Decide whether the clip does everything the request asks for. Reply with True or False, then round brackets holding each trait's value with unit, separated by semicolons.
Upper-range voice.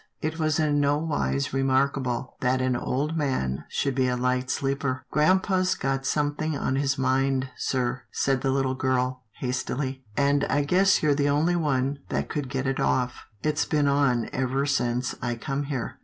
False (135 Hz)